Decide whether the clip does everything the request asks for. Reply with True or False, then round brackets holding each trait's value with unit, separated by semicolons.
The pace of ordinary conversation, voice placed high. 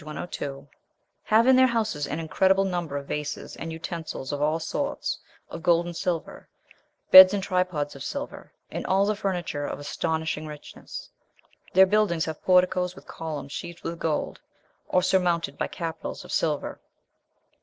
False (155 wpm; 170 Hz)